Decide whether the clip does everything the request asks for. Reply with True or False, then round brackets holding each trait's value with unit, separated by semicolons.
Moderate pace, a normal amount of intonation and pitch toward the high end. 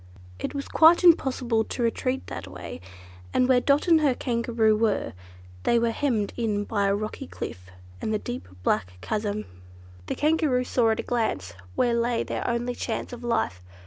True (175 wpm; 3.4 semitones; 235 Hz)